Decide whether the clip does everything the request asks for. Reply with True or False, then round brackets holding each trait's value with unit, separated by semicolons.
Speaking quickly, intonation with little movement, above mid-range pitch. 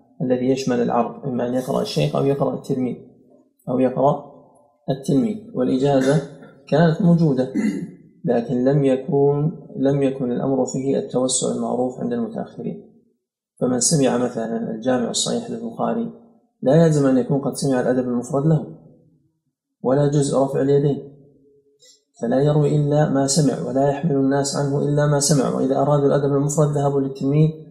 False (140 wpm; 2.2 semitones; 140 Hz)